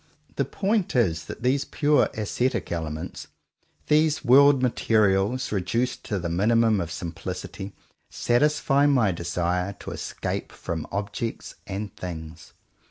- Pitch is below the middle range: Yes, low, 105 Hz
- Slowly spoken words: Yes, slow, 120 wpm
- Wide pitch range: Yes, wide, 6.4 semitones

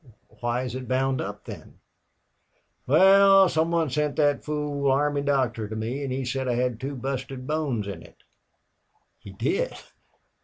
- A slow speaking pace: No, average, 160 wpm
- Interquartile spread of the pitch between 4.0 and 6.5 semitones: No, average, 3.1 semitones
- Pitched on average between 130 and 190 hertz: Yes, low, 135 Hz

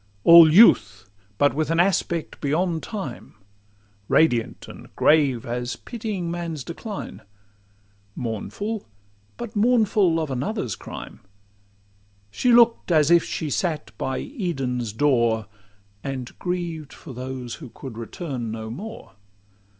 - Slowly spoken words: Yes, slow, 110 wpm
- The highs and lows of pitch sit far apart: Yes, wide, 6.6 semitones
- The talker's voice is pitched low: No, medium, 150 Hz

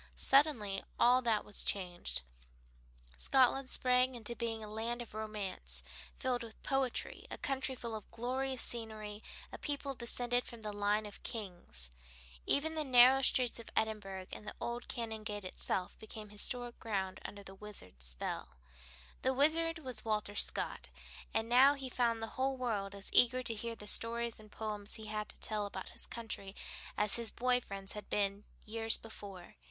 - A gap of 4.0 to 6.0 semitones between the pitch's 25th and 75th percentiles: No, average, 3.2 semitones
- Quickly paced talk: No, average, 170 wpm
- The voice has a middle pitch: No, high, 225 Hz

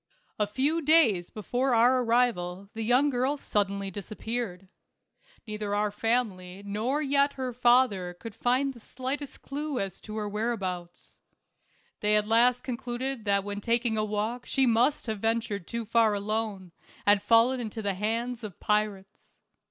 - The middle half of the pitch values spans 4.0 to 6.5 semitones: No, average, 3.4 semitones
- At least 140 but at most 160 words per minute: Yes, average, 150 wpm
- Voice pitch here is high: Yes, high, 225 Hz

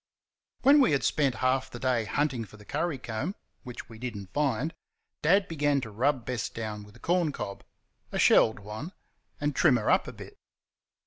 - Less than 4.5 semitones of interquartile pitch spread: No, average, 5.0 semitones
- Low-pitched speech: Yes, low, 130 Hz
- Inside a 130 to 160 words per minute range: No, average, 195 wpm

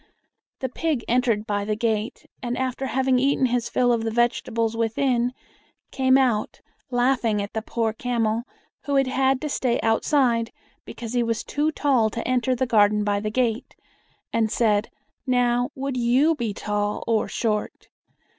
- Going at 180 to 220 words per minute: No, average, 165 wpm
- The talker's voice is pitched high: Yes, high, 240 Hz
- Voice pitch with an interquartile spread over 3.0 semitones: No, average, 2.7 semitones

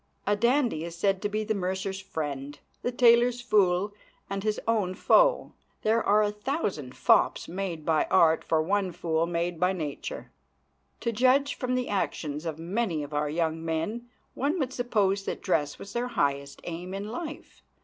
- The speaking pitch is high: Yes, high, 195 Hz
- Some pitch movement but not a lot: No, wide, 6.0 semitones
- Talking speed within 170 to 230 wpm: Yes, average, 175 wpm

